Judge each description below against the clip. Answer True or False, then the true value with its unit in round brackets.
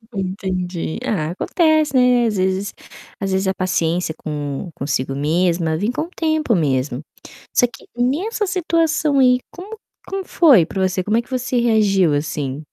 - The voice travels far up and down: True (8.0 semitones)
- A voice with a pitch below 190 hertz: False (195 Hz)